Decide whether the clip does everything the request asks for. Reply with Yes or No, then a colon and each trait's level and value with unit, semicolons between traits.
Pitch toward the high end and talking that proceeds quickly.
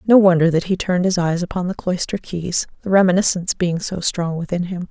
No: medium, 180 Hz; fast, 220 wpm